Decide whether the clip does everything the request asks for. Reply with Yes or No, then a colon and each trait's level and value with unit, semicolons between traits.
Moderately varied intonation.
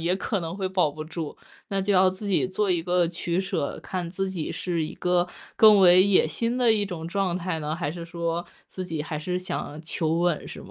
No: narrow, 2.3 semitones